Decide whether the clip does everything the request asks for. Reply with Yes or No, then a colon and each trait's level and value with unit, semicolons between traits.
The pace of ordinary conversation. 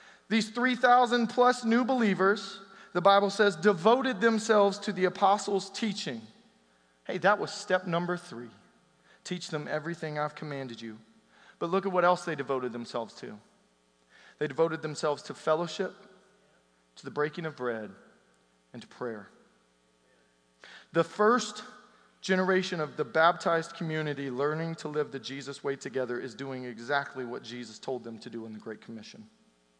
Yes: average, 150 wpm